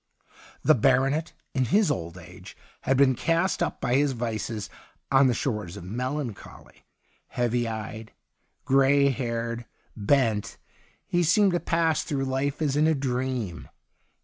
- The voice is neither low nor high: No, low, 130 Hz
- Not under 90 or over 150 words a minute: Yes, average, 140 wpm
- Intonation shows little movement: No, average, 3.8 semitones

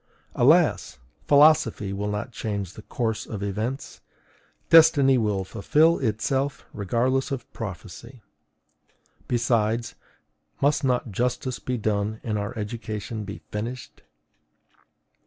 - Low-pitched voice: Yes, low, 115 Hz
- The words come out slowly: Yes, slow, 105 wpm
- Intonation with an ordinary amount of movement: Yes, average, 3.7 semitones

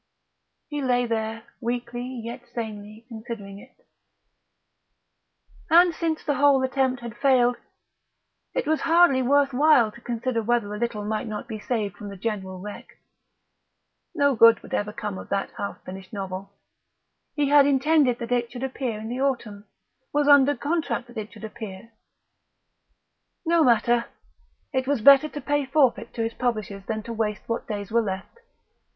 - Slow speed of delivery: No, average, 160 wpm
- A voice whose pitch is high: Yes, high, 240 Hz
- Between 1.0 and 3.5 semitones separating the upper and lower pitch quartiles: No, average, 4.2 semitones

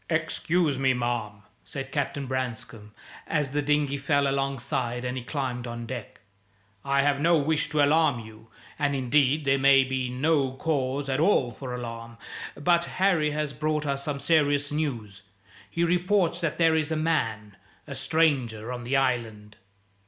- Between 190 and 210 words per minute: No, average, 160 wpm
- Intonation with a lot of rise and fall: No, average, 3.6 semitones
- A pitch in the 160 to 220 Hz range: No, medium, 140 Hz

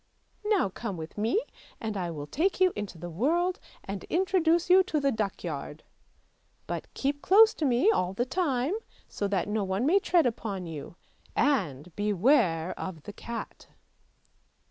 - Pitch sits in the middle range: No, high, 225 Hz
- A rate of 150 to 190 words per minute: Yes, average, 160 wpm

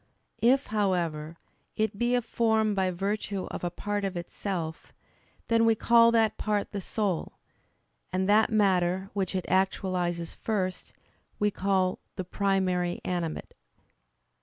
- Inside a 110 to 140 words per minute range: Yes, slow, 135 wpm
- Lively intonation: No, average, 2.9 semitones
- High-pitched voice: Yes, high, 195 Hz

